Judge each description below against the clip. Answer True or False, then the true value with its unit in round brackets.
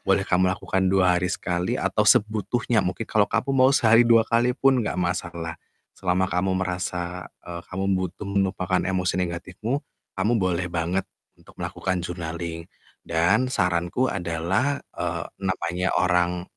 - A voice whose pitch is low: True (95 Hz)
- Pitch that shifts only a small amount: False (3.0 semitones)